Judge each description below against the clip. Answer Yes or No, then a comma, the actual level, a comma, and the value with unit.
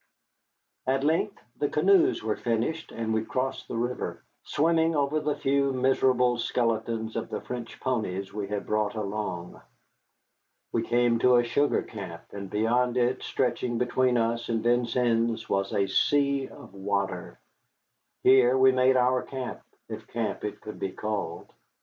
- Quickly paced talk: No, average, 150 wpm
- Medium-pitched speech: No, low, 120 Hz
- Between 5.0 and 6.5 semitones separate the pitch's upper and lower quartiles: No, average, 3.2 semitones